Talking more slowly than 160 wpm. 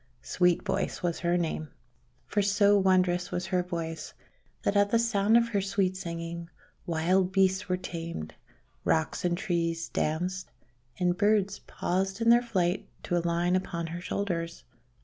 Yes: average, 150 wpm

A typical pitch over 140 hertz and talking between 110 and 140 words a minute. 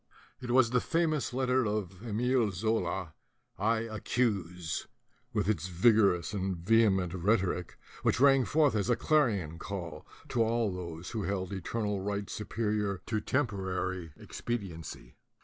No: low, 105 Hz; slow, 135 wpm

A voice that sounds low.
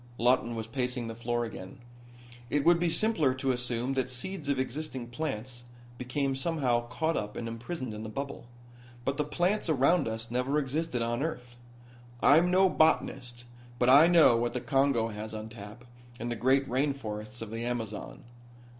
Yes: low, 125 Hz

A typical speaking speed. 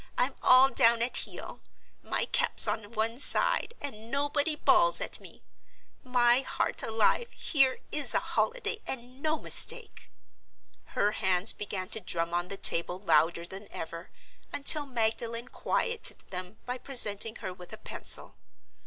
Yes: average, 145 wpm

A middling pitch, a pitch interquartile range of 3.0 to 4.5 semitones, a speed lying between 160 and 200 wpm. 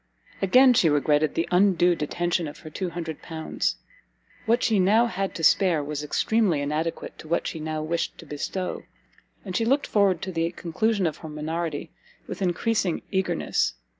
Yes: medium, 170 Hz; average, 3.7 semitones; average, 165 wpm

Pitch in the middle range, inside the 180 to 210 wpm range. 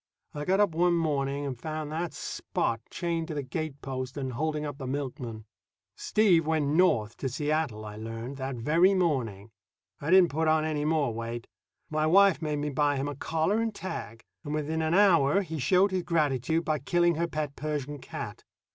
Yes: medium, 150 Hz; average, 190 wpm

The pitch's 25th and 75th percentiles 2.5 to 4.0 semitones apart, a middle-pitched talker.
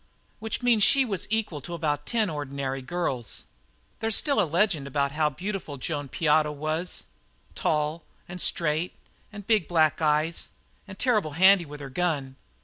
No: average, 4.9 semitones; medium, 160 Hz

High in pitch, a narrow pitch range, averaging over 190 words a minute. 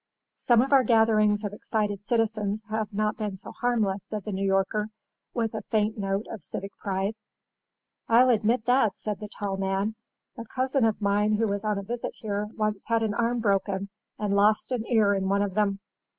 Yes: high, 210 Hz; narrow, 2.0 semitones; average, 200 wpm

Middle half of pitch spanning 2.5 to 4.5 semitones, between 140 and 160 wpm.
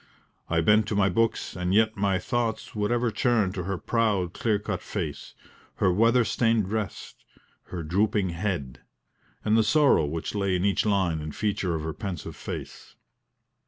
No: average, 3.6 semitones; average, 170 wpm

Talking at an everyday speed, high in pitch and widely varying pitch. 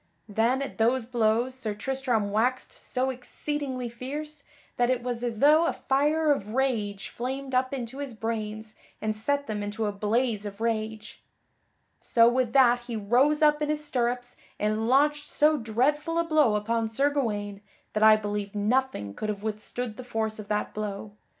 No: average, 175 wpm; high, 240 Hz; average, 3.8 semitones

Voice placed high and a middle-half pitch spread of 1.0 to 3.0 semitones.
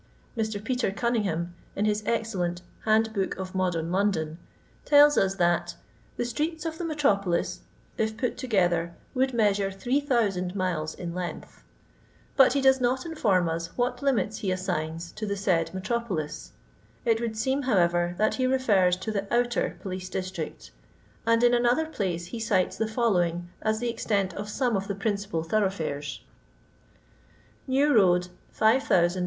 No: high, 205 Hz; average, 4.9 semitones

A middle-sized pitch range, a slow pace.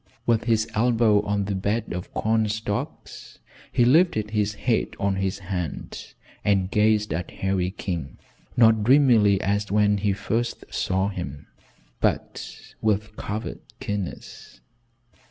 No: narrow, 2.3 semitones; slow, 130 wpm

